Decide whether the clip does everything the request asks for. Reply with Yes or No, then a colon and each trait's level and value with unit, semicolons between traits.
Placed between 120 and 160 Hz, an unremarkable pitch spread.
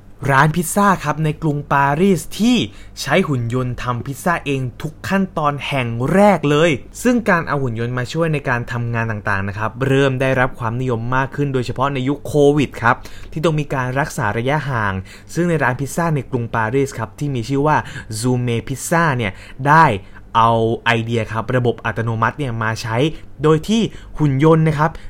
Yes: low, 135 Hz; average, 4.8 semitones